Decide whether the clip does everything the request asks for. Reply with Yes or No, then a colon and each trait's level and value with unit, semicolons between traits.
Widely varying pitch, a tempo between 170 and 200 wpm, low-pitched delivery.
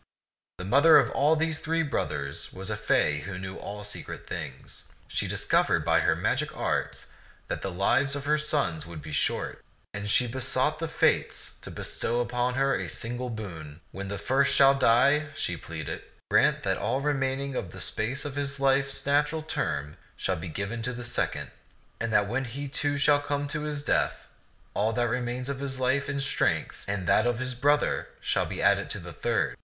Yes: wide, 5.7 semitones; average, 195 wpm; low, 125 Hz